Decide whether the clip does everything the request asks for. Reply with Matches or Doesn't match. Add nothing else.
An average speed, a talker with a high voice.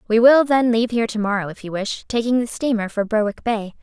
Doesn't match